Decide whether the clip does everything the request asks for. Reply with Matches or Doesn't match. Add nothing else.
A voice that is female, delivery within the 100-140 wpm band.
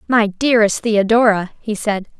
Matches